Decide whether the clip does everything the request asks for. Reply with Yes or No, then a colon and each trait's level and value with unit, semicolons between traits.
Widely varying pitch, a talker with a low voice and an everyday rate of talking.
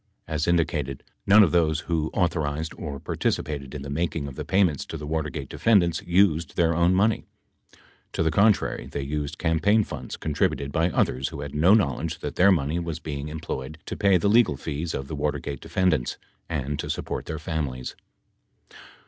No: average, 3.2 semitones; very low, 80 Hz; average, 180 wpm